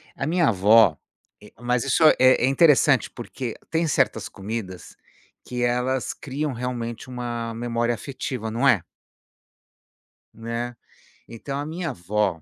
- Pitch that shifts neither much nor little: Yes, average, 3.2 semitones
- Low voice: Yes, low, 120 Hz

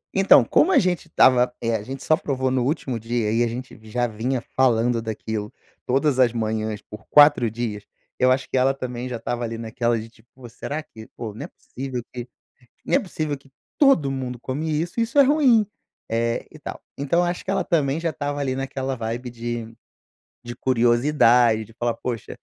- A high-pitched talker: No, low, 125 Hz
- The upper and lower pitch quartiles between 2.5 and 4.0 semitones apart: Yes, average, 3.6 semitones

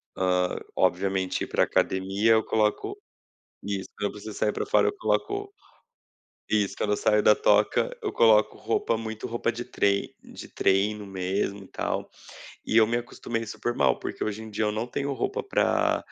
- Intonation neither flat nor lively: No, narrow, 2.3 semitones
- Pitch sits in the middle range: No, low, 105 Hz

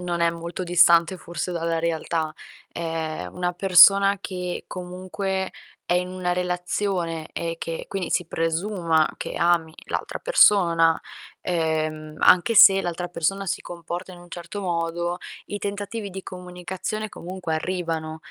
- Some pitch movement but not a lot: No, narrow, 2.0 semitones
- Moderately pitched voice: Yes, medium, 175 Hz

